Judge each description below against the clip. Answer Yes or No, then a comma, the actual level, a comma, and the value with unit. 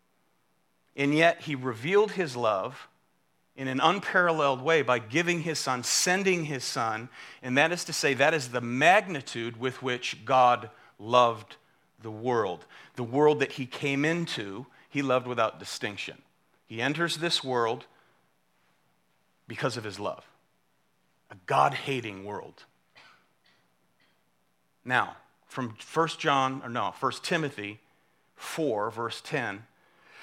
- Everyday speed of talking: No, slow, 130 wpm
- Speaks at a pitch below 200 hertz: Yes, low, 135 Hz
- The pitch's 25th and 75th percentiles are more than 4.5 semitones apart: Yes, average, 4.9 semitones